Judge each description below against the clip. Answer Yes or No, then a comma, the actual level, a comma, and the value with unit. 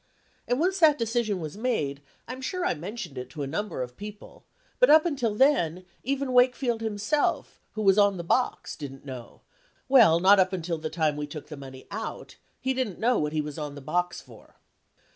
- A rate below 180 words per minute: No, average, 200 wpm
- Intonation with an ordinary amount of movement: No, wide, 8.5 semitones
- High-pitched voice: Yes, high, 200 Hz